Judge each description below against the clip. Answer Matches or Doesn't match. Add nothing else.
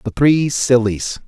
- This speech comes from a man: Matches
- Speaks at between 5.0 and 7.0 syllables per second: Doesn't match